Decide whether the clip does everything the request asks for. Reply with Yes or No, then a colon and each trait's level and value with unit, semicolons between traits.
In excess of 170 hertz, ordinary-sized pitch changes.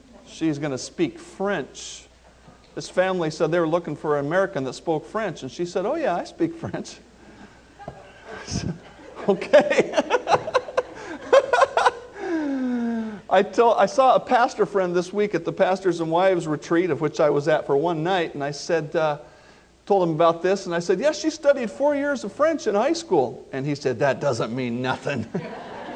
No: high, 190 Hz; wide, 7.9 semitones